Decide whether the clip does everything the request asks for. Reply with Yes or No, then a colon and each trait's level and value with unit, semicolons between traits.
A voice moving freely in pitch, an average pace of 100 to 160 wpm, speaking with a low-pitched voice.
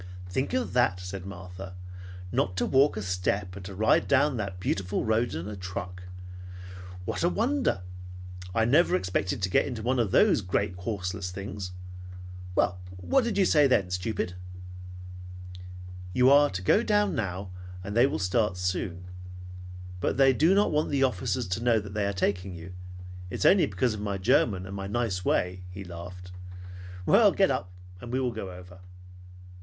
No: wide, 5.7 semitones; average, 175 wpm; low, 100 Hz